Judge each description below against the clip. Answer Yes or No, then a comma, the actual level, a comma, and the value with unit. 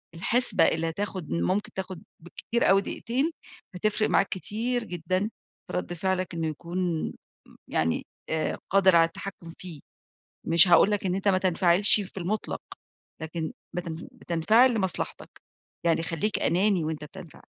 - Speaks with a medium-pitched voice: Yes, medium, 180 Hz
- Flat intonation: No, average, 3.3 semitones